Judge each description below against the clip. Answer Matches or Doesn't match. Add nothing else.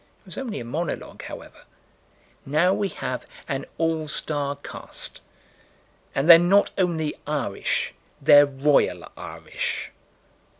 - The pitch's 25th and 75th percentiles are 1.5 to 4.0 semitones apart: Matches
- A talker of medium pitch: Matches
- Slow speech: Matches